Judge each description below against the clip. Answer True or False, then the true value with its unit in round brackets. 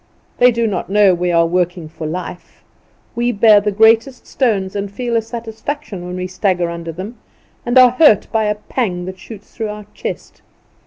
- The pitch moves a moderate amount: True (4.1 semitones)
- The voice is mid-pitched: False (205 Hz)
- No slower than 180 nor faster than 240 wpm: True (190 wpm)